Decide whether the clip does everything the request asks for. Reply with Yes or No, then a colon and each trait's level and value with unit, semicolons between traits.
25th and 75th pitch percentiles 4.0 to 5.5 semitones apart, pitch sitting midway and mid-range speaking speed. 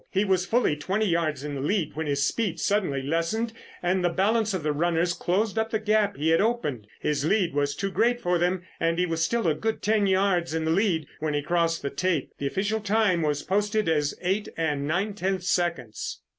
No: average, 4.7 semitones; medium, 175 Hz; fast, 220 wpm